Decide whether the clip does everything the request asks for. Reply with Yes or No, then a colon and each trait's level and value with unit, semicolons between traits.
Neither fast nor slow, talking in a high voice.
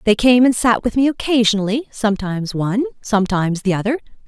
Yes: average, 170 wpm; high, 225 Hz